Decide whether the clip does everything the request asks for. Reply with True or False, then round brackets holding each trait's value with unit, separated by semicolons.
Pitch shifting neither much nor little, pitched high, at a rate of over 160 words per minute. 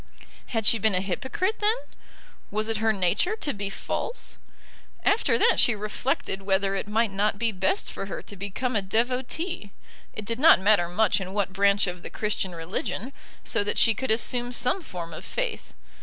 True (4.0 semitones; 210 Hz; 185 wpm)